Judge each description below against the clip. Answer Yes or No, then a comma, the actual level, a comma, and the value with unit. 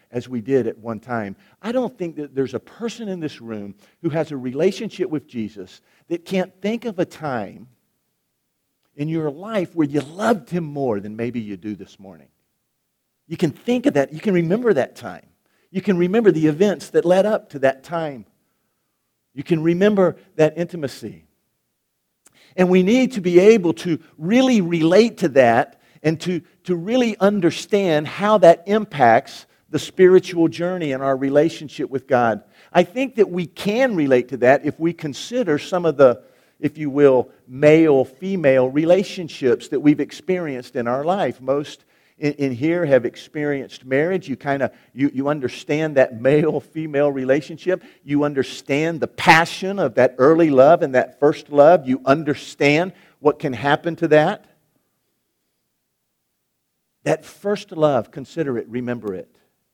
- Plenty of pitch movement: No, average, 5.0 semitones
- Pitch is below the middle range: No, medium, 155 Hz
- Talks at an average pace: Yes, average, 165 wpm